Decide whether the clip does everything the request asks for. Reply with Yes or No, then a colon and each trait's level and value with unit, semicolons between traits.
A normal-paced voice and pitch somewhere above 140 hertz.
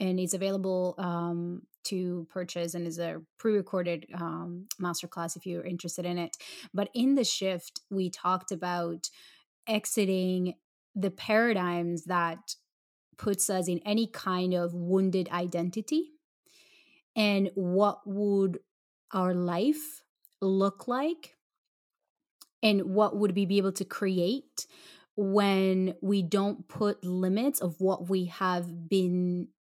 No: slow, 120 wpm; high, 190 Hz